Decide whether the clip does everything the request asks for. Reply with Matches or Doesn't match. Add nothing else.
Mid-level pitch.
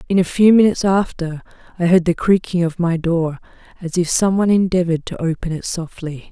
Matches